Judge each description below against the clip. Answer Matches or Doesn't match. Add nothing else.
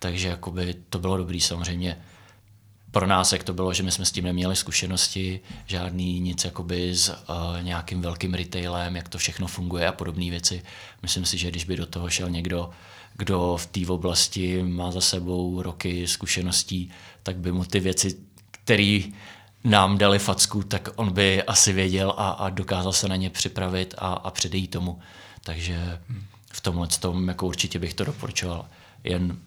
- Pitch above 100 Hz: Doesn't match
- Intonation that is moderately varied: Doesn't match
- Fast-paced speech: Matches